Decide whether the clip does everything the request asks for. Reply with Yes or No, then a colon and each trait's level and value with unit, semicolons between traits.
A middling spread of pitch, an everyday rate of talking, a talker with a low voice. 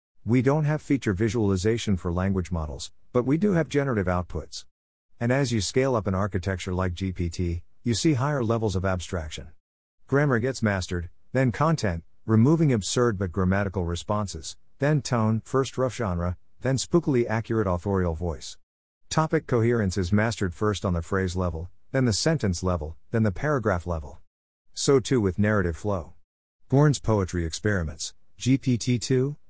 No: wide, 5.7 semitones; average, 155 wpm; low, 100 Hz